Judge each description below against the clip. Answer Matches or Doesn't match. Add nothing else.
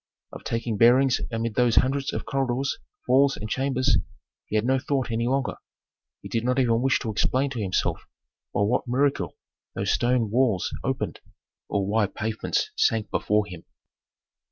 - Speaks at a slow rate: Doesn't match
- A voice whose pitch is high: Doesn't match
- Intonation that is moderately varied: Matches